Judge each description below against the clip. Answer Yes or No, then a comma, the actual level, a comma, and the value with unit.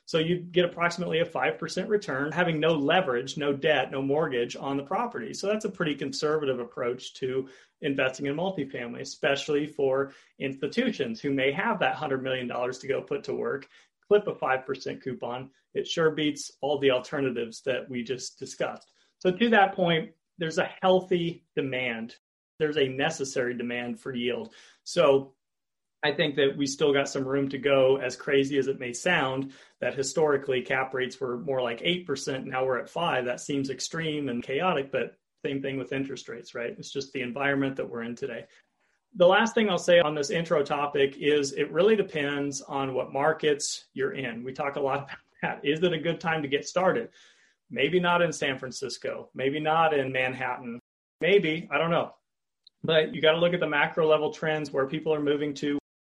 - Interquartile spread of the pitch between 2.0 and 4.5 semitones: Yes, average, 3.8 semitones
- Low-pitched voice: No, medium, 145 Hz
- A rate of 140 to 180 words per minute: No, average, 190 wpm